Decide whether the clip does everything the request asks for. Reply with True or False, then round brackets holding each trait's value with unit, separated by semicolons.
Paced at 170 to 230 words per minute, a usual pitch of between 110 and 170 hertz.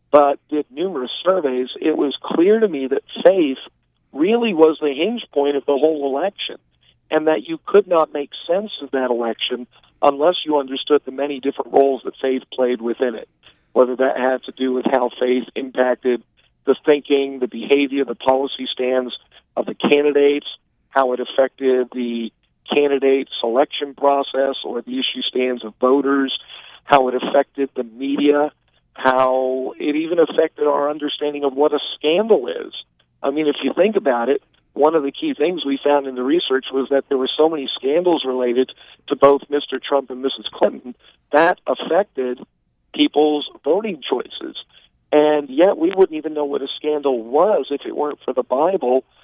True (175 wpm; 140 Hz)